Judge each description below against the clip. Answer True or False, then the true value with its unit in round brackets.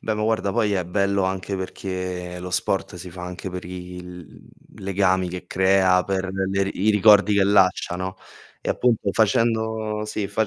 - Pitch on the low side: True (95 Hz)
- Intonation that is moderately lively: False (2.2 semitones)